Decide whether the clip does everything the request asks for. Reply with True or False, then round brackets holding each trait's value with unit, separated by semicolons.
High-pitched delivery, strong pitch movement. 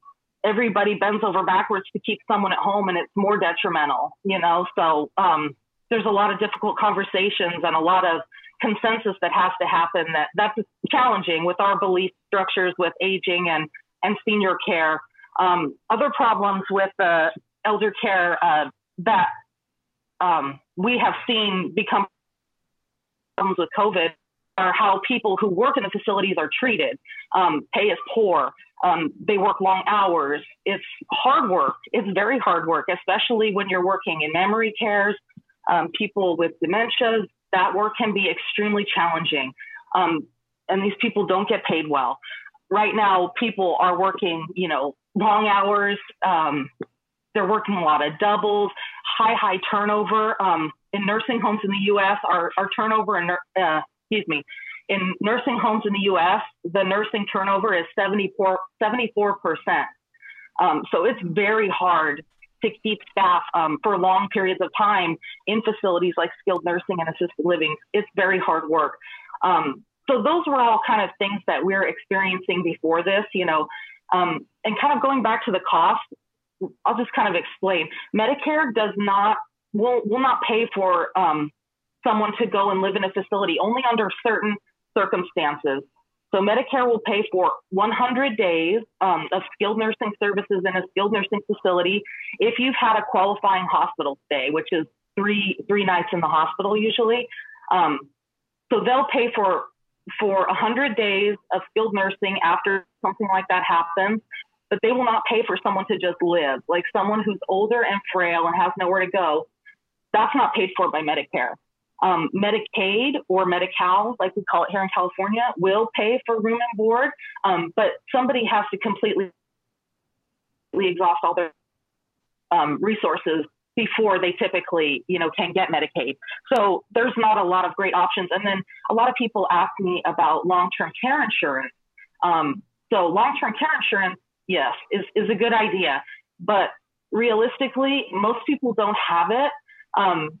False (200 Hz; 3.4 semitones)